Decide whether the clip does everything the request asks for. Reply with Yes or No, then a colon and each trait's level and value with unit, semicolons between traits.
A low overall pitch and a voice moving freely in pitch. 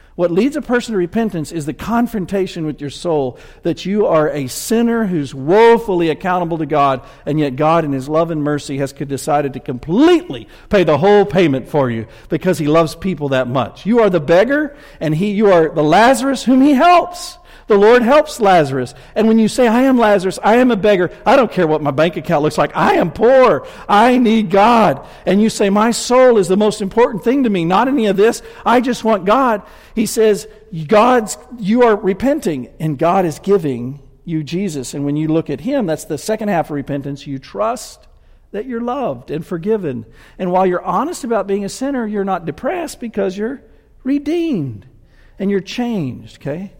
No: high, 190 Hz; wide, 7.2 semitones